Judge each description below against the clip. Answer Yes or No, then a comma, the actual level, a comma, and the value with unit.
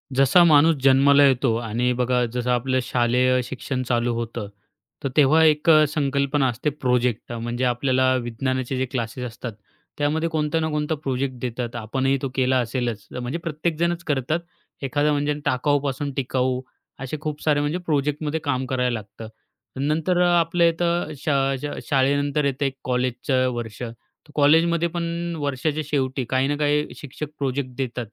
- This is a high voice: No, low, 135 Hz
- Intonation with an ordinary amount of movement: Yes, average, 3.0 semitones